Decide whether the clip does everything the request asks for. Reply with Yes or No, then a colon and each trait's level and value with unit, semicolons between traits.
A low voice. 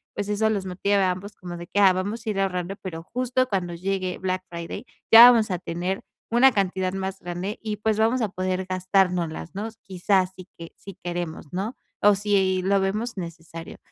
No: high, 190 Hz